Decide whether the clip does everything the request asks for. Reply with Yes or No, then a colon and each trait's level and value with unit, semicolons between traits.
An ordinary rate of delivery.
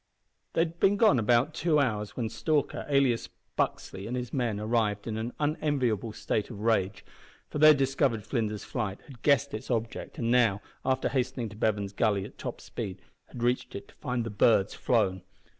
Yes: average, 190 wpm